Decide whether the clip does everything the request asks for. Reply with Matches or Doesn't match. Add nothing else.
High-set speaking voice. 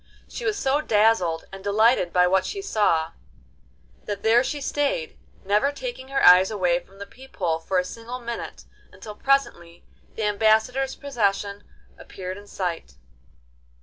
Matches